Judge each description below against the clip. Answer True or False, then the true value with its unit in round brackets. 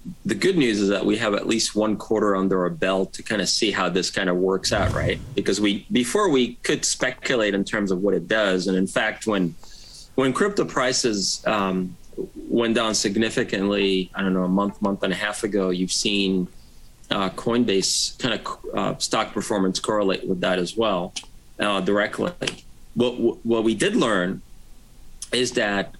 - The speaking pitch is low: True (100 Hz)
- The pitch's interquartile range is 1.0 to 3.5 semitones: True (2.9 semitones)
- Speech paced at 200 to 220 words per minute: False (185 wpm)